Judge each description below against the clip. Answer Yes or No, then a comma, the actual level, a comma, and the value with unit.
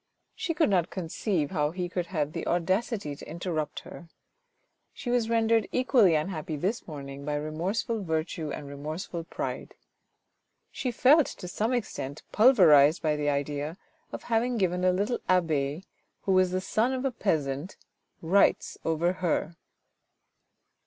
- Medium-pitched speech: Yes, medium, 175 Hz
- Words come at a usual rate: Yes, average, 150 wpm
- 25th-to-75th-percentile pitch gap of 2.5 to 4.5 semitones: No, wide, 5.6 semitones